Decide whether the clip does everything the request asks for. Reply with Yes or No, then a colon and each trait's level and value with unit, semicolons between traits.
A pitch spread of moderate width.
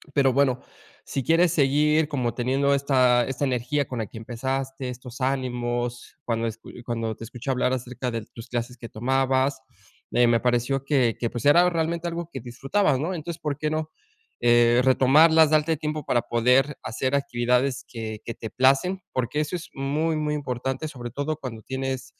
Yes: average, 3.4 semitones